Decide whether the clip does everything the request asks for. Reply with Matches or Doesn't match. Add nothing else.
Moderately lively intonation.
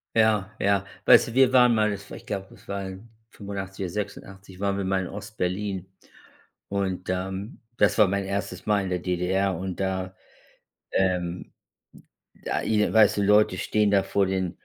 Doesn't match